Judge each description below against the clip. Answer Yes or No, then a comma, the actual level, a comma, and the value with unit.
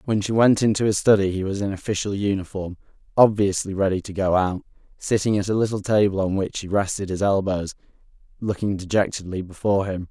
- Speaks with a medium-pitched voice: No, low, 100 Hz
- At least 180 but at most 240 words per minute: Yes, average, 185 wpm